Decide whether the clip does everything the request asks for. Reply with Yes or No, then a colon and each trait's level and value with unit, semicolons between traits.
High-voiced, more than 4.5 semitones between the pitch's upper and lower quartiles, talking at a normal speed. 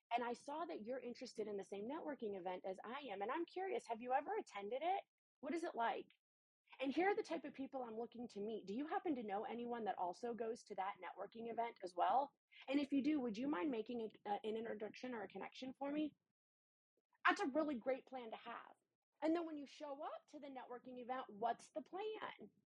No: very high, 255 Hz; average, 5.0 semitones; fast, 235 wpm